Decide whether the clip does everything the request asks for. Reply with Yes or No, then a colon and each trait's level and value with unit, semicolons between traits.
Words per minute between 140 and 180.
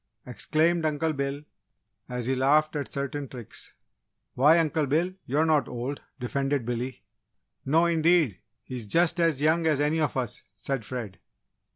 Yes: average, 155 wpm